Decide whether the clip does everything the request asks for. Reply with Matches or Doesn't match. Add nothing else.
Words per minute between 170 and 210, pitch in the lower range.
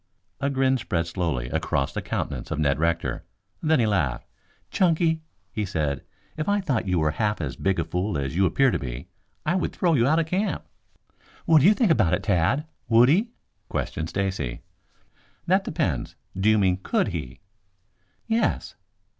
Matches